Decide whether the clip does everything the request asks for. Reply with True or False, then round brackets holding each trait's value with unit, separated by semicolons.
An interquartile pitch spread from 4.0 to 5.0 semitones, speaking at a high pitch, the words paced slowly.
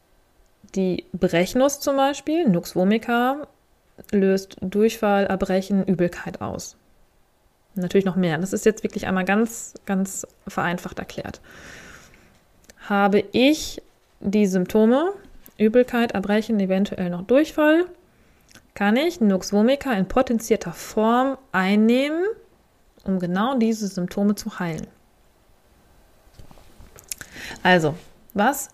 True (4.6 semitones; 205 Hz; 100 wpm)